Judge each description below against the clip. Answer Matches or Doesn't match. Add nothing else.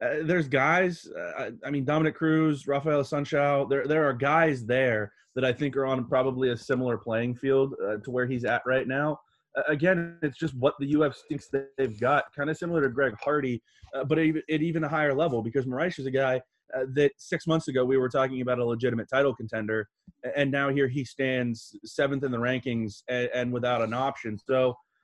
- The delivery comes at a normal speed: Doesn't match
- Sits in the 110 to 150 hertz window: Matches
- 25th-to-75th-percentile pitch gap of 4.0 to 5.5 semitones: Doesn't match